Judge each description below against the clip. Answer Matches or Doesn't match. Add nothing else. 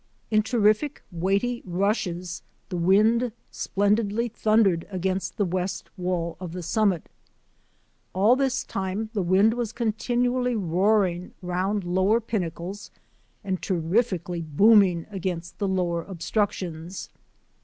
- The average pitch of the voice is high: Matches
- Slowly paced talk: Matches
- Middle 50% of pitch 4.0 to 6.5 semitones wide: Doesn't match